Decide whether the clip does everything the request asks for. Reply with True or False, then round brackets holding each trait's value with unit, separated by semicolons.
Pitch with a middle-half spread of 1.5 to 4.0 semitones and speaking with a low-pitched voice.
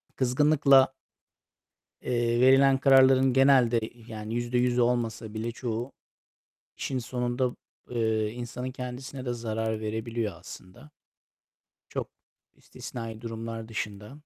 True (2.6 semitones; 120 Hz)